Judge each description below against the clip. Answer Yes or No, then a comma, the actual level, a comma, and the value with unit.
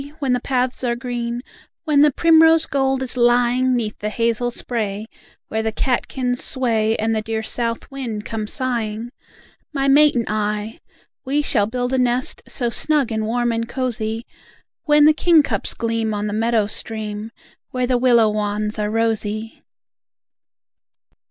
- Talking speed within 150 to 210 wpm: Yes, average, 160 wpm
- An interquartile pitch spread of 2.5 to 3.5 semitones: Yes, average, 2.8 semitones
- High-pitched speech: Yes, high, 235 Hz